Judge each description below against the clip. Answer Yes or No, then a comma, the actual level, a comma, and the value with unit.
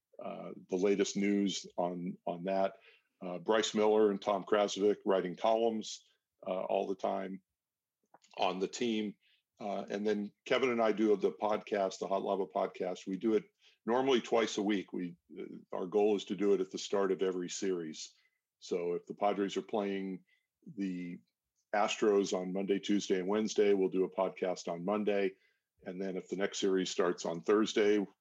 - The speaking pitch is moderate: No, low, 100 Hz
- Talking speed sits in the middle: Yes, average, 180 wpm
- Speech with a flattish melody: Yes, narrow, 1.8 semitones